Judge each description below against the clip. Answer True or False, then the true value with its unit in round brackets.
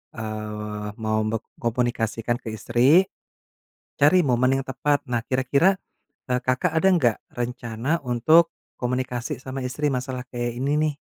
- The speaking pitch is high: False (125 Hz)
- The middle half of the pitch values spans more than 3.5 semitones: False (3.1 semitones)